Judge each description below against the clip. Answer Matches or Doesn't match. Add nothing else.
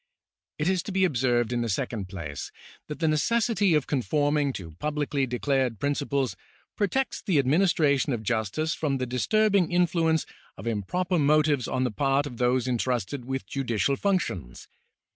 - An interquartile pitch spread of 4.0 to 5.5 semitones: Matches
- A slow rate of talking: Doesn't match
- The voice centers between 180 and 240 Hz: Doesn't match